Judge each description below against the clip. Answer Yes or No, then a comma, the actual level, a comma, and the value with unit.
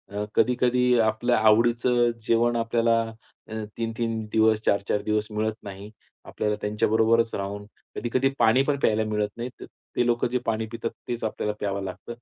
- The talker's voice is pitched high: No, low, 115 Hz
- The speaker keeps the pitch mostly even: Yes, narrow, 1.9 semitones